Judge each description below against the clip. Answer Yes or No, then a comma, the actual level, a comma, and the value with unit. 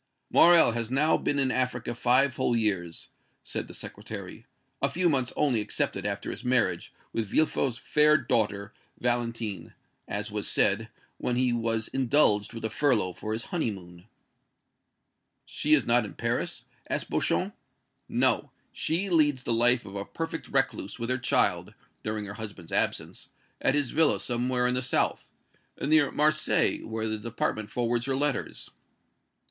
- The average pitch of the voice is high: No, low, 120 Hz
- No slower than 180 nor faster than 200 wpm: No, average, 155 wpm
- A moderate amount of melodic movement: Yes, average, 3.9 semitones